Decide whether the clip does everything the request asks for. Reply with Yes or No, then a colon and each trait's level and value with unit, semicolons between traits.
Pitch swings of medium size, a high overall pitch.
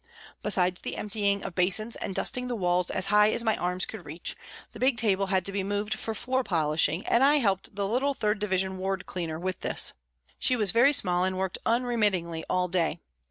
Yes: average, 3.5 semitones; high, 195 Hz